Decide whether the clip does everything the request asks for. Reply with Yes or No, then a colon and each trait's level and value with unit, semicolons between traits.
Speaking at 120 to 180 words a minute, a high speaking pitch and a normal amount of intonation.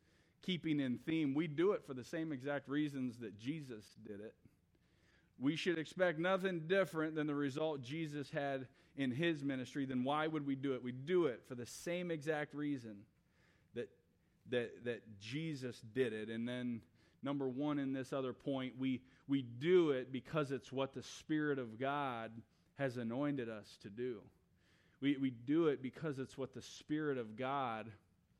No: average, 175 wpm; low, 135 Hz; average, 3.6 semitones